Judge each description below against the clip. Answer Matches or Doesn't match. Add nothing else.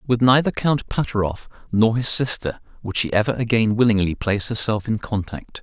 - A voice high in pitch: Doesn't match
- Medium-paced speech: Matches